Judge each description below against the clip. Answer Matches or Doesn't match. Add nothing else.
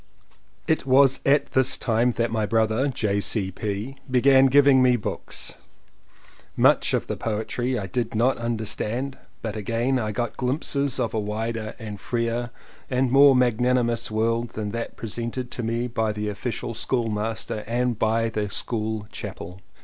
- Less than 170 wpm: Matches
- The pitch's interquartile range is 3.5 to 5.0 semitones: Doesn't match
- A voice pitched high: Doesn't match